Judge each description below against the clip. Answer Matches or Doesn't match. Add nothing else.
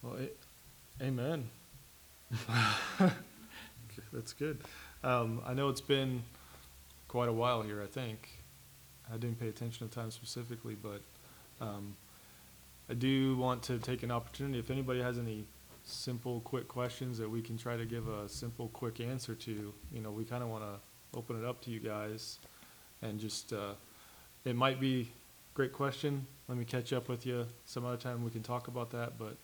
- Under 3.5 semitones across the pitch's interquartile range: Matches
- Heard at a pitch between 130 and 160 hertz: Doesn't match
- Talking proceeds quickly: Doesn't match